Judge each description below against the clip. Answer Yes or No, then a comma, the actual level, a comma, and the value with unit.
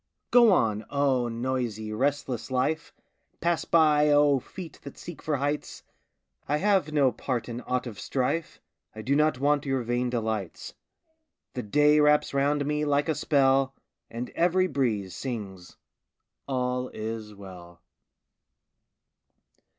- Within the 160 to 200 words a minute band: No, slow, 135 wpm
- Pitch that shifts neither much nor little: Yes, average, 4.1 semitones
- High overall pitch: No, low, 135 Hz